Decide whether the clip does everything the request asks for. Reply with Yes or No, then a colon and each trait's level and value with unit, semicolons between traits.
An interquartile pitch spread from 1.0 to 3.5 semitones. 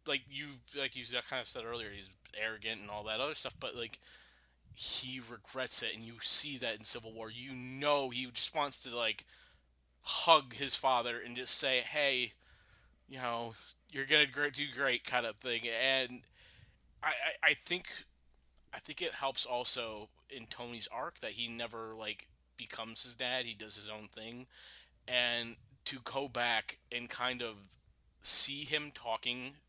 Yes: average, 2.9 semitones